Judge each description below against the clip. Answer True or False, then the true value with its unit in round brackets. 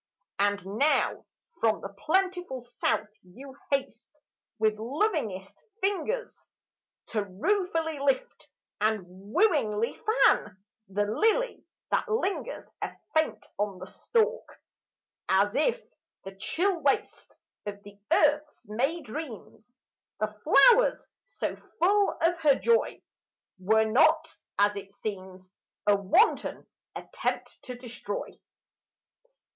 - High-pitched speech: True (250 Hz)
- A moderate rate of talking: False (110 wpm)